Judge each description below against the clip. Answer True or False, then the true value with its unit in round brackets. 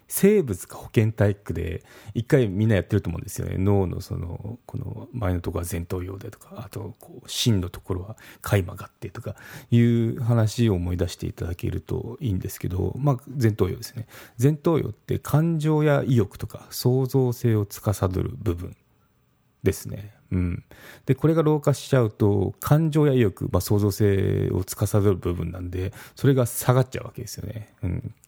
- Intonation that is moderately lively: True (4.5 semitones)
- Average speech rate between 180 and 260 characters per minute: False (345 characters per minute)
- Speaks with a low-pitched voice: True (110 Hz)